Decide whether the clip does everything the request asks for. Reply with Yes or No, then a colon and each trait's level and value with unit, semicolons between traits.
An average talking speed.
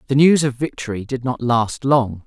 No: fast, 210 wpm